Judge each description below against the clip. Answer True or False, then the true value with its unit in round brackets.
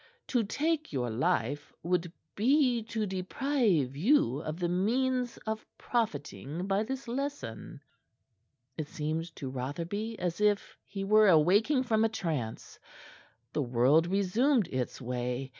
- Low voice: False (190 Hz)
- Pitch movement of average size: False (7.8 semitones)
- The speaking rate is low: True (130 wpm)